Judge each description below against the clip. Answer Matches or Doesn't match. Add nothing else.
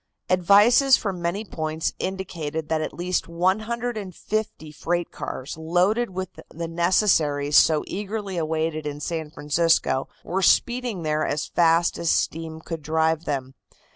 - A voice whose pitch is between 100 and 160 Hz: Doesn't match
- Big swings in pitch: Doesn't match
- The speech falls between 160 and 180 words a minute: Doesn't match